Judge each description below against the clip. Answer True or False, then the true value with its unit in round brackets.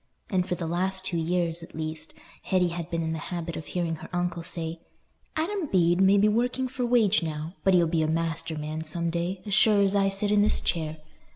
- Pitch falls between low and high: True (175 Hz)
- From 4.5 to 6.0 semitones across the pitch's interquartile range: False (3.2 semitones)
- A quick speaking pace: True (225 wpm)